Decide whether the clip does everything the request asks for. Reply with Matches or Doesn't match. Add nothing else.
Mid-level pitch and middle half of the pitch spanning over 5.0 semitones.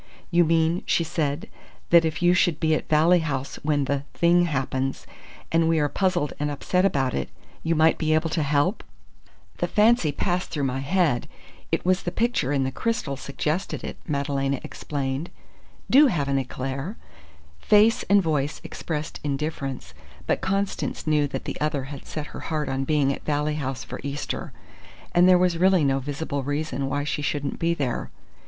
Doesn't match